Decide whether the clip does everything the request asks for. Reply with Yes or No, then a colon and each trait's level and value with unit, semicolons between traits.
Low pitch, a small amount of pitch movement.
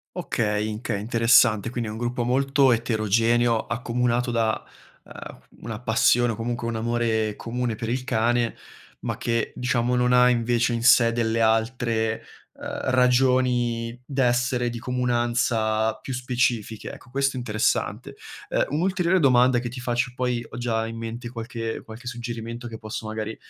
Yes: low, 120 Hz; narrow, 1.6 semitones